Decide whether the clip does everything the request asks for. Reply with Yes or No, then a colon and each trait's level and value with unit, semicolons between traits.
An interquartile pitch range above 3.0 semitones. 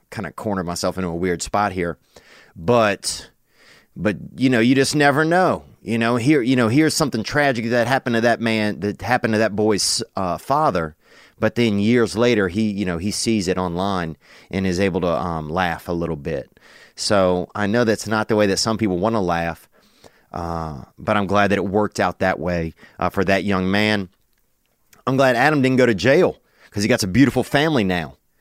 Yes: average, 4.6 semitones